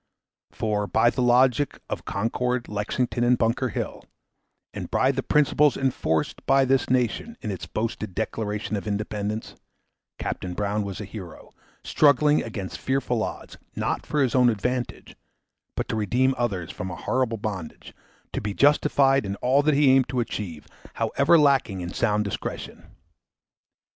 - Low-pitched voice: Yes, low, 115 Hz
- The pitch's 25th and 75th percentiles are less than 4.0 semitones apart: No, average, 4.3 semitones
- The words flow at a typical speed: Yes, average, 160 wpm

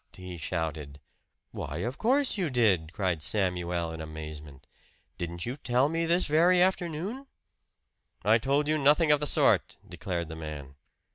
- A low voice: Yes, low, 105 Hz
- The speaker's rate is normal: Yes, average, 150 wpm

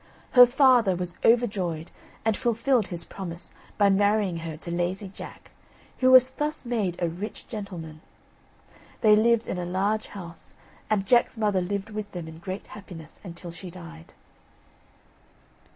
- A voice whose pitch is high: Yes, high, 195 Hz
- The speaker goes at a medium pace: Yes, average, 150 wpm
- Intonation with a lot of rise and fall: No, average, 4.1 semitones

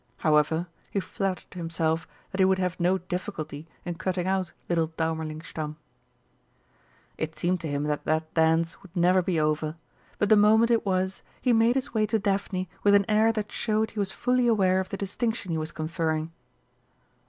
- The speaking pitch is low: No, medium, 185 Hz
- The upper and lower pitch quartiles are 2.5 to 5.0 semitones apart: Yes, average, 4.0 semitones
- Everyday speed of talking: Yes, average, 180 wpm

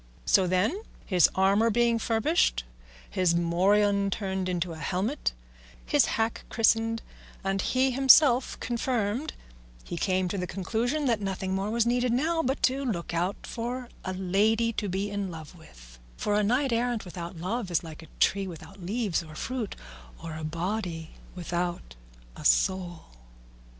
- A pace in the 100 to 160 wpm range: Yes, average, 155 wpm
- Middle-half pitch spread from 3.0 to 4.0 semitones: No, average, 4.8 semitones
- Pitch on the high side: Yes, high, 200 Hz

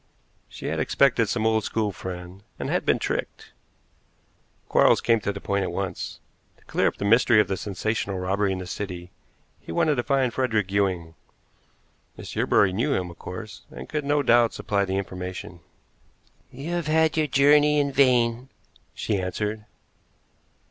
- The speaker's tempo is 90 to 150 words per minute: No, average, 170 wpm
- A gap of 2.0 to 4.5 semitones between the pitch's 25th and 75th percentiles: No, wide, 5.4 semitones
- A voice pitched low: Yes, low, 105 Hz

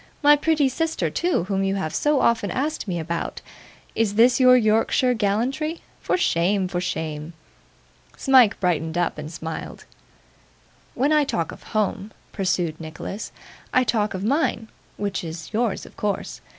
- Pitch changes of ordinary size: No, wide, 6.4 semitones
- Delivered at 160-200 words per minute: No, average, 150 wpm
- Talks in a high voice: Yes, high, 210 Hz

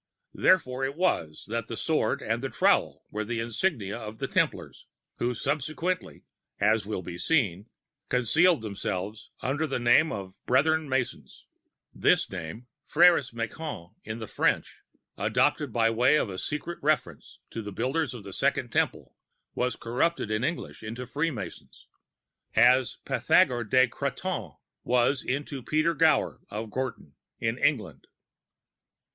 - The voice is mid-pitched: No, low, 125 Hz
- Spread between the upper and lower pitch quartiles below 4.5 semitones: No, wide, 5.4 semitones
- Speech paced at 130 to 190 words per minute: Yes, average, 140 wpm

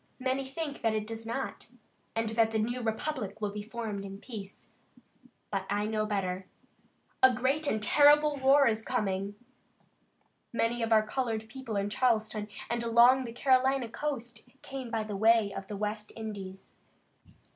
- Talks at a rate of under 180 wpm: Yes, average, 155 wpm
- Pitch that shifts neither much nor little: Yes, average, 3.5 semitones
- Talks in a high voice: Yes, high, 225 Hz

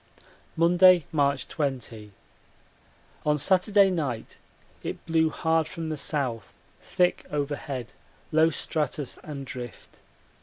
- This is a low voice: No, medium, 150 Hz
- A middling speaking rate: No, slow, 105 wpm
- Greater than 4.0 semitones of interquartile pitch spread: No, average, 3.3 semitones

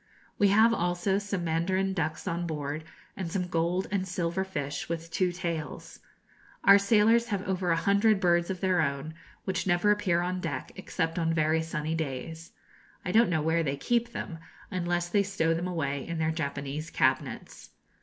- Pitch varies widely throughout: No, average, 2.9 semitones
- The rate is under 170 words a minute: No, average, 180 wpm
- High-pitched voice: No, medium, 175 Hz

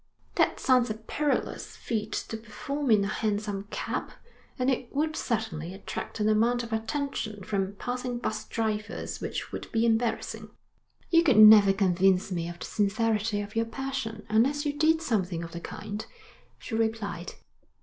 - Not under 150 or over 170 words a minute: Yes, average, 160 wpm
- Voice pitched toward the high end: Yes, high, 220 Hz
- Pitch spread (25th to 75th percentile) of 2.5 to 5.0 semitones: Yes, average, 3.2 semitones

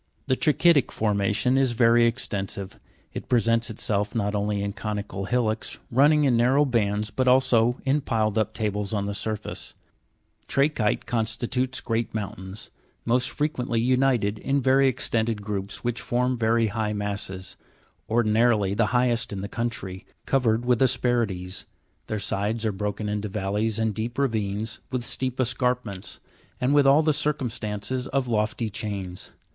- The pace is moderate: Yes, average, 150 wpm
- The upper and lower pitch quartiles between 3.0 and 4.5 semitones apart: Yes, average, 3.3 semitones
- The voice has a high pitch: No, low, 115 Hz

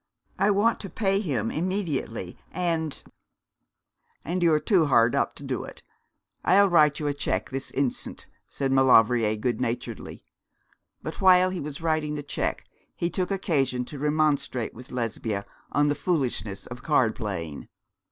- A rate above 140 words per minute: Yes, average, 155 wpm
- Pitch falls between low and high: Yes, medium, 145 Hz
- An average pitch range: No, wide, 5.9 semitones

